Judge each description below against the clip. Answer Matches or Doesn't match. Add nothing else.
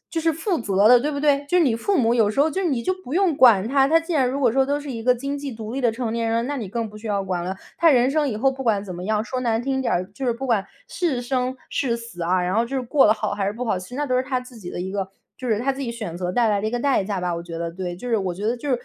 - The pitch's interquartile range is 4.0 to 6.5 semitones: Matches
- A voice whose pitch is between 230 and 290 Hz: Matches